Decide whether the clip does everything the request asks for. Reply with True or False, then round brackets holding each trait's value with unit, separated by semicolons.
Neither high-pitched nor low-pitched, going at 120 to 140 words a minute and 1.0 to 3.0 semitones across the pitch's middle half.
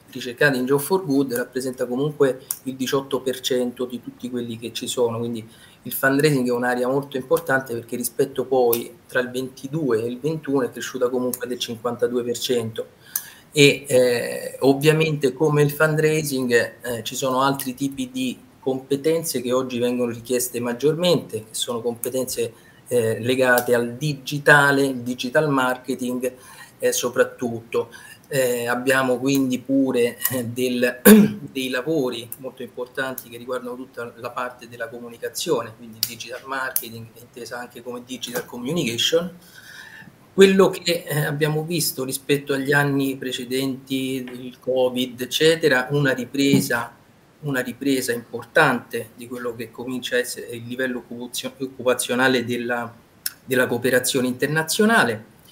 False (130 Hz; 130 wpm; 2.6 semitones)